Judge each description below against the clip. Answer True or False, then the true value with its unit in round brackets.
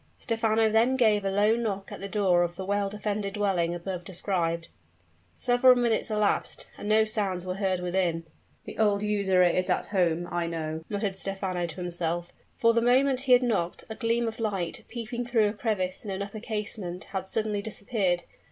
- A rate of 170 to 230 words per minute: True (190 wpm)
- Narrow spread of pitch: False (3.5 semitones)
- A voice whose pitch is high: True (200 Hz)